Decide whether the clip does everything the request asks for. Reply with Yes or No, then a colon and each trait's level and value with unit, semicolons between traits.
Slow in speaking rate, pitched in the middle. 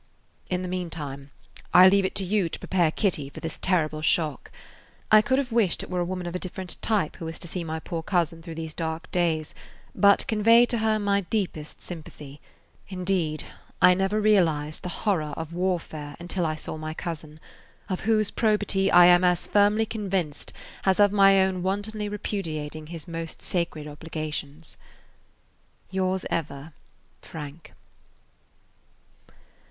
No: average, 160 wpm; medium, 175 Hz